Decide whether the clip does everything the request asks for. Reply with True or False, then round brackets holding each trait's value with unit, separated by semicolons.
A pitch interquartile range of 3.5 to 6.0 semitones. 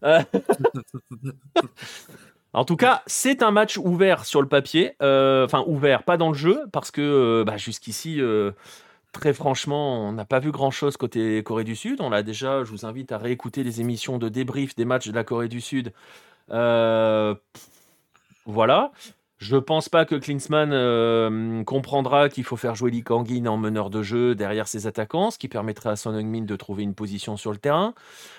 True (4.4 semitones)